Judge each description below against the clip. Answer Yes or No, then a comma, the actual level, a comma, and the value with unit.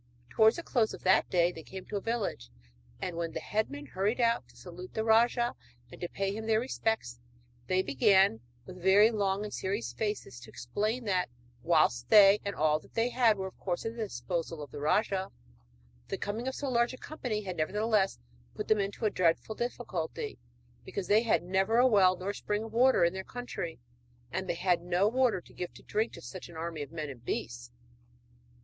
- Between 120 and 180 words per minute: No, fast, 205 wpm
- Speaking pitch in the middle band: No, high, 195 Hz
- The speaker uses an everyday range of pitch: Yes, average, 4.4 semitones